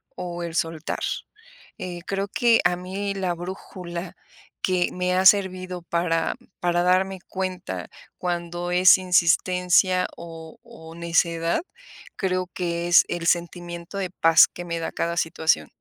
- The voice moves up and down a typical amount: No, narrow, 1.4 semitones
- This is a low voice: No, medium, 175 Hz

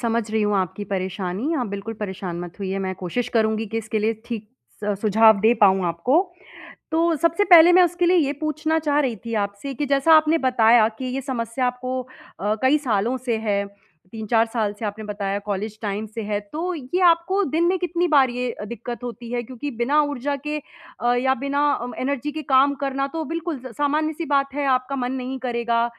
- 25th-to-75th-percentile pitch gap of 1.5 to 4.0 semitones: No, average, 5.1 semitones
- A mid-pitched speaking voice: No, high, 245 Hz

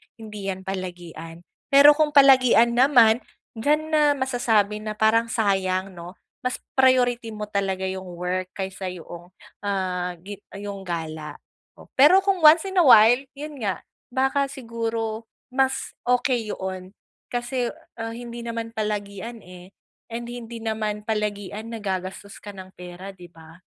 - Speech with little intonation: No, average, 4.5 semitones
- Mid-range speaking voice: No, high, 215 Hz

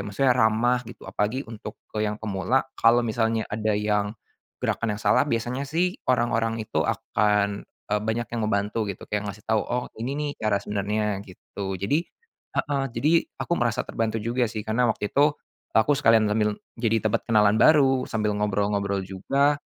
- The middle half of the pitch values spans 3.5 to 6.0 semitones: No, average, 3.0 semitones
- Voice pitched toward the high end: No, low, 110 Hz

